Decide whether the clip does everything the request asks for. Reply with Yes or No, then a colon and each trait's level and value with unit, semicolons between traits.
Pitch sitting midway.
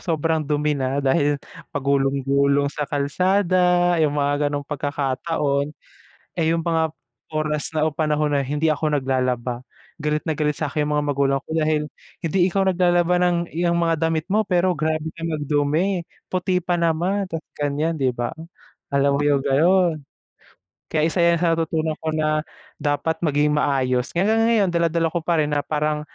Yes: medium, 155 Hz